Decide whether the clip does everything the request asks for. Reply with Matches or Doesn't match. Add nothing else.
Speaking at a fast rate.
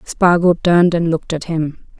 Doesn't match